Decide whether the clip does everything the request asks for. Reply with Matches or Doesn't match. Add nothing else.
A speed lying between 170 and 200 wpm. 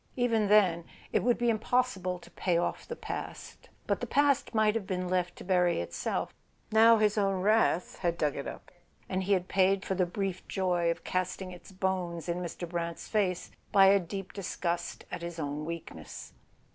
Matches